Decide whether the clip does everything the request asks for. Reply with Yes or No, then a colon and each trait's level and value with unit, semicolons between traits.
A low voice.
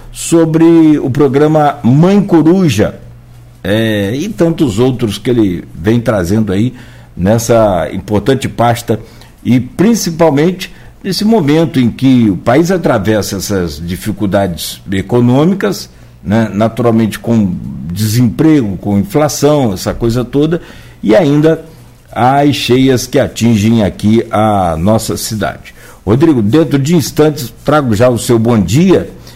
Yes: low, 120 Hz